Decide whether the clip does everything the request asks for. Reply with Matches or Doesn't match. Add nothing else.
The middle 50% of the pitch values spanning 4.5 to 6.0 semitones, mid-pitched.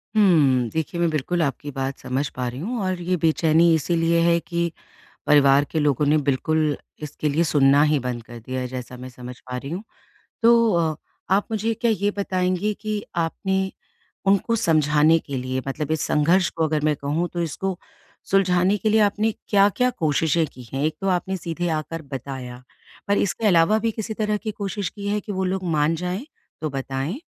Matches